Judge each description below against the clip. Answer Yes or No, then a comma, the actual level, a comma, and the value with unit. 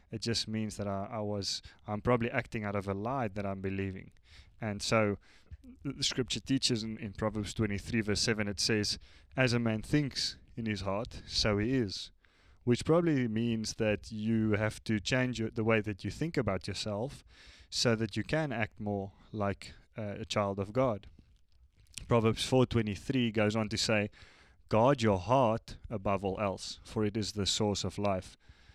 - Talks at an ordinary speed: Yes, average, 180 wpm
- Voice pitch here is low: Yes, low, 105 Hz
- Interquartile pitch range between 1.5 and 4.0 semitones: Yes, average, 2.7 semitones